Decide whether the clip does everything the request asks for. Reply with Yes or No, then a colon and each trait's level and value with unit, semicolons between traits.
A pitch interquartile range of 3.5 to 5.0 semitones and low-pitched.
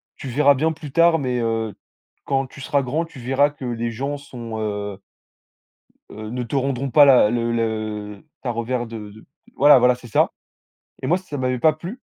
Yes: average, 3.9 semitones; low, 125 Hz